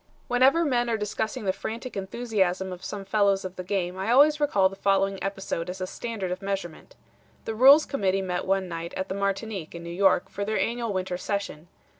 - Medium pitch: No, high, 195 Hz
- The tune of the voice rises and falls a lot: No, average, 3.0 semitones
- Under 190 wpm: No, fast, 205 wpm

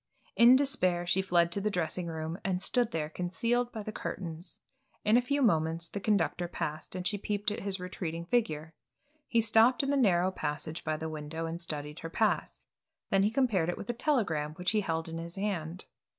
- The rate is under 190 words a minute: No, fast, 205 wpm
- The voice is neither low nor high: Yes, medium, 180 Hz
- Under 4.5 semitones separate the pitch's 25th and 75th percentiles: No, average, 4.8 semitones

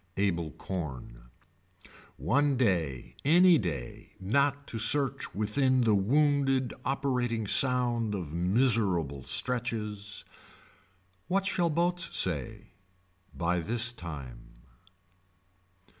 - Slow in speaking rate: Yes, slow, 90 wpm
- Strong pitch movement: Yes, wide, 7.9 semitones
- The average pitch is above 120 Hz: No, low, 110 Hz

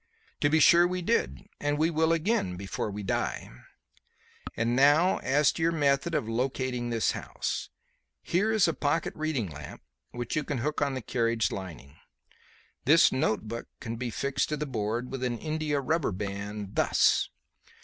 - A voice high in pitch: No, low, 130 Hz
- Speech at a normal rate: Yes, average, 170 wpm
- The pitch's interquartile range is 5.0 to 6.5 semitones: Yes, wide, 5.6 semitones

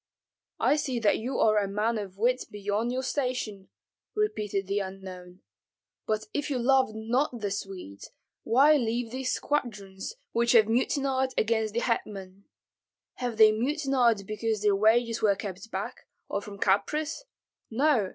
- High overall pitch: Yes, high, 220 Hz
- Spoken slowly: No, average, 150 wpm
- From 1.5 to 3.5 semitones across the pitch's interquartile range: No, average, 4.1 semitones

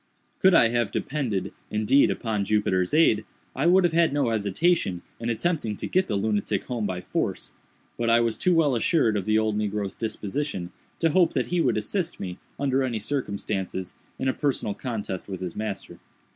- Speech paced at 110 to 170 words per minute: No, average, 185 wpm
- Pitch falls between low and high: No, low, 115 Hz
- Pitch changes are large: Yes, wide, 6.0 semitones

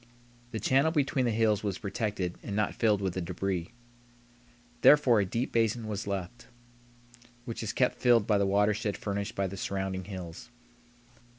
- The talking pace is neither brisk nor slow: Yes, average, 165 wpm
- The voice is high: No, low, 105 Hz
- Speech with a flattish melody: No, average, 3.0 semitones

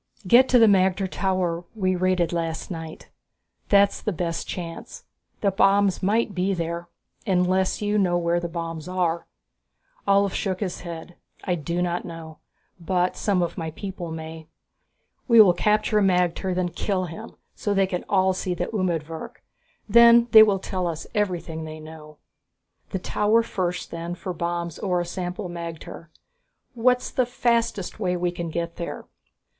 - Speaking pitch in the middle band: Yes, medium, 180 Hz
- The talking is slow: No, average, 160 wpm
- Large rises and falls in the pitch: No, average, 2.7 semitones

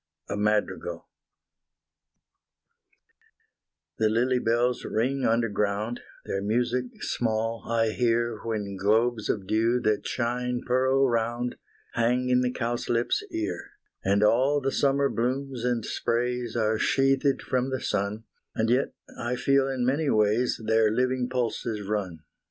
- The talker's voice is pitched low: Yes, low, 120 Hz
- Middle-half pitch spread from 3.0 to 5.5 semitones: No, narrow, 2.5 semitones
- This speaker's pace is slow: Yes, slow, 130 wpm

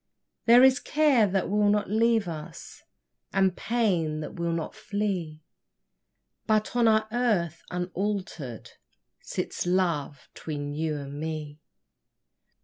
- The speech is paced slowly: Yes, slow, 120 wpm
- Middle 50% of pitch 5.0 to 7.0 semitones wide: Yes, wide, 5.6 semitones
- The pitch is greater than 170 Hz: Yes, medium, 185 Hz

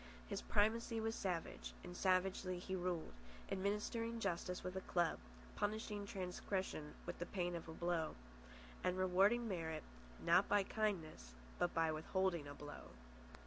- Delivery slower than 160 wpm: Yes, average, 145 wpm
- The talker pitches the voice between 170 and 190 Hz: Yes, medium, 185 Hz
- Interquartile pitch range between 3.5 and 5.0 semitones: No, average, 3.1 semitones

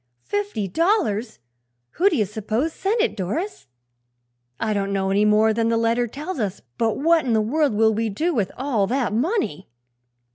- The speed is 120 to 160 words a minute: No, average, 180 wpm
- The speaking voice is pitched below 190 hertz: No, high, 225 Hz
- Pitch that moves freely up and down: Yes, wide, 6.6 semitones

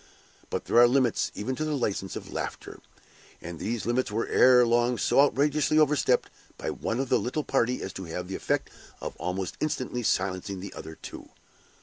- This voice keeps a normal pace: Yes, average, 190 wpm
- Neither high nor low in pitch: No, low, 120 Hz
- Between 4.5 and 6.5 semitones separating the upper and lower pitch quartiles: Yes, wide, 5.4 semitones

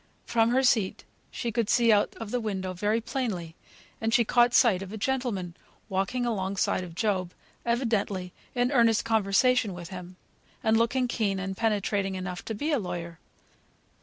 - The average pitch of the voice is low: No, high, 215 Hz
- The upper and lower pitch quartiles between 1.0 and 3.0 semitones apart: No, average, 3.9 semitones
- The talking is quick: No, average, 165 wpm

